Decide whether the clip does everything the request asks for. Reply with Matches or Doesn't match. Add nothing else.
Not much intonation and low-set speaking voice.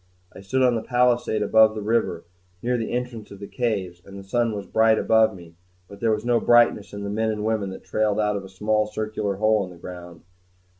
Matches